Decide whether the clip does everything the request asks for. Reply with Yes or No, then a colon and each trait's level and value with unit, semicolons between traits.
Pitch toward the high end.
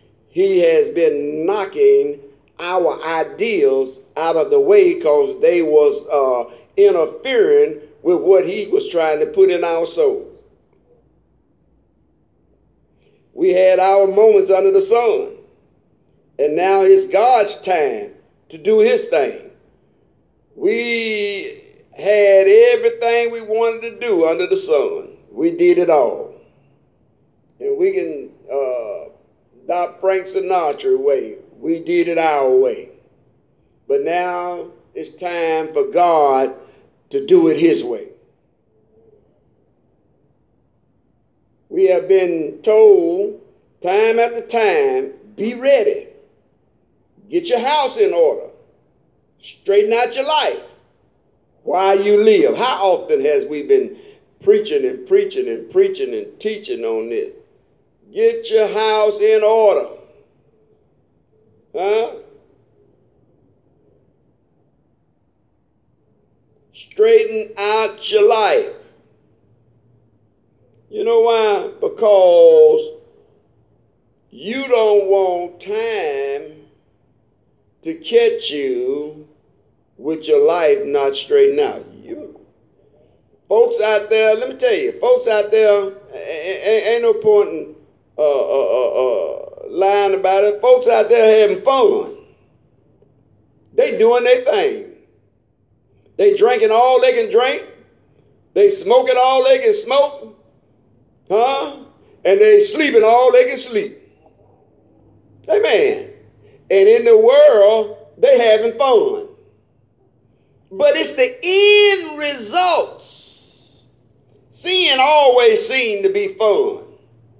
Yes: very high, 400 Hz